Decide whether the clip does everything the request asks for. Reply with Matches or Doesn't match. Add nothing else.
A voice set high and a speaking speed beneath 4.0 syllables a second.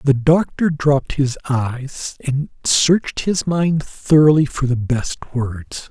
Doesn't match